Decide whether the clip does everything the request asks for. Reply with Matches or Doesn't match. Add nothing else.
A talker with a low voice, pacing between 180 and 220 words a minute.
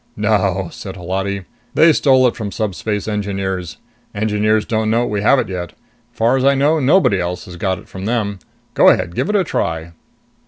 Matches